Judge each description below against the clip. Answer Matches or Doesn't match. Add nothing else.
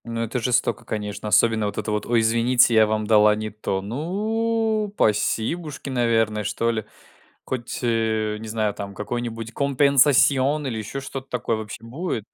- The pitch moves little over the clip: Doesn't match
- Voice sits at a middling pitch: Doesn't match